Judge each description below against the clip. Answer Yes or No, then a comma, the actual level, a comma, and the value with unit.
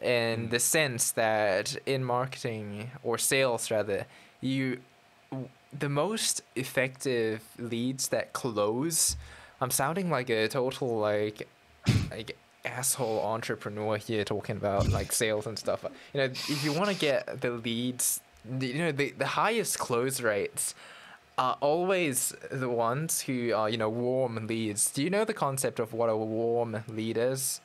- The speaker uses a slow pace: No, average, 150 wpm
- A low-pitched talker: Yes, low, 120 Hz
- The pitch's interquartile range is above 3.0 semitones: Yes, average, 3.5 semitones